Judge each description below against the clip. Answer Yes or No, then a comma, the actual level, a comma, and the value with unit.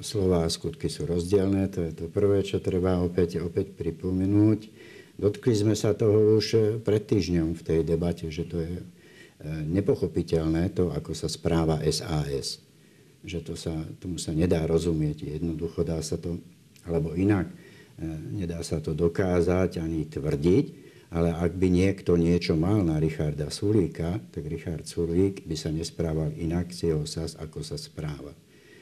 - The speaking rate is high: No, average, 155 wpm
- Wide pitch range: No, average, 2.8 semitones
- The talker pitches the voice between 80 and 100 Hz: Yes, very low, 85 Hz